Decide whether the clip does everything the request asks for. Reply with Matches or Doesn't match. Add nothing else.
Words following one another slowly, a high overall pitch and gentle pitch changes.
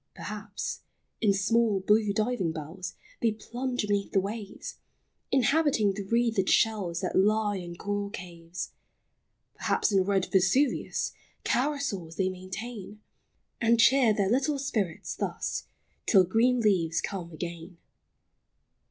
Doesn't match